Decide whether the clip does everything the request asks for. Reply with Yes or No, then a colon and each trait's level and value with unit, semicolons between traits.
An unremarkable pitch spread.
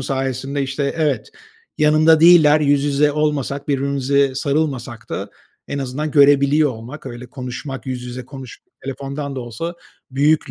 No: narrow, 2.1 semitones